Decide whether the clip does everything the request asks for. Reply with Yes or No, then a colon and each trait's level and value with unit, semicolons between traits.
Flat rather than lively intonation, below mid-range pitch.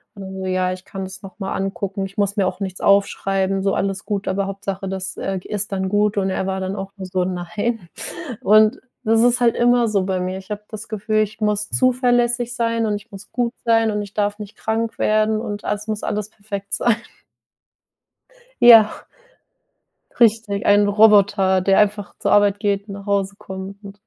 No: narrow, 2.0 semitones; high, 205 Hz